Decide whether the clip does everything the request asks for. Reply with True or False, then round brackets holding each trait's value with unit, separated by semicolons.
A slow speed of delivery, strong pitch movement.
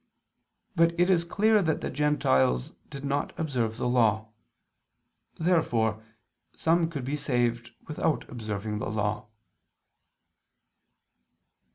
True (105 wpm; 6.7 semitones)